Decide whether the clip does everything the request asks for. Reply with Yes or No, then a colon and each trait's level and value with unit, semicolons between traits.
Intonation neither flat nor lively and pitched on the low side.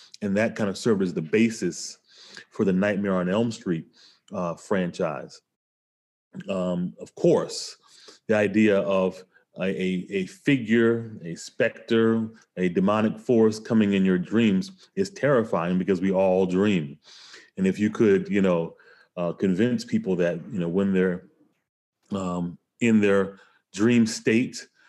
Yes: average, 3.4 semitones; low, 100 Hz